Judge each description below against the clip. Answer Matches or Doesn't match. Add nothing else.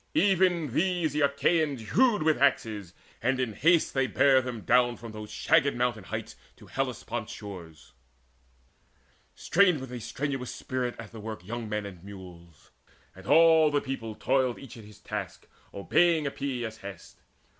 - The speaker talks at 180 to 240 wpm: Doesn't match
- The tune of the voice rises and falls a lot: Matches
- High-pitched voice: Doesn't match